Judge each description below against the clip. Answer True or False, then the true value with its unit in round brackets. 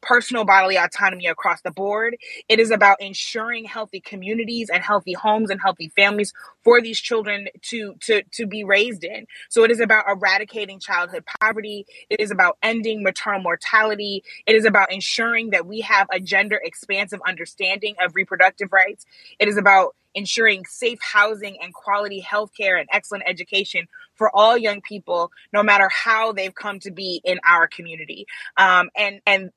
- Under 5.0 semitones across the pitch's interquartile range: True (2.4 semitones)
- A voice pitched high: True (205 Hz)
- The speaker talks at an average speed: True (170 wpm)